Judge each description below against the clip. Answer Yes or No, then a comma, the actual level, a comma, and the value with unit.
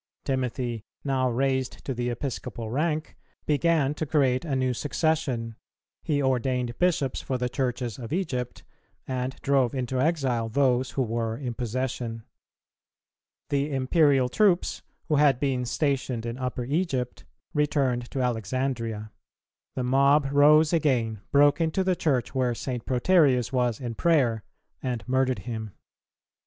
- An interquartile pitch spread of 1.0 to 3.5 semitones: Yes, average, 2.8 semitones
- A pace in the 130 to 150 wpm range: Yes, average, 140 wpm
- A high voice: No, low, 130 Hz